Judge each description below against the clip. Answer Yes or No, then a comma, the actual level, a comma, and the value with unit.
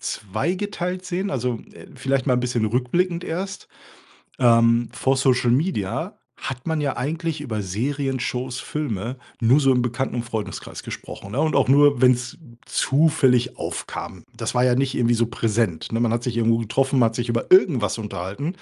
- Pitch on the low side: Yes, low, 125 Hz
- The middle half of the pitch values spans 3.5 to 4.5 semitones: Yes, average, 3.8 semitones